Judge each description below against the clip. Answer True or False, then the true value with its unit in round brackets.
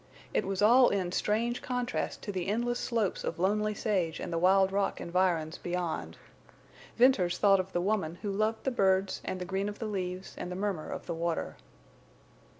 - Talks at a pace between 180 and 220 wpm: True (190 wpm)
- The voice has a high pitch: True (195 Hz)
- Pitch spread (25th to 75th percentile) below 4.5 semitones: True (2.9 semitones)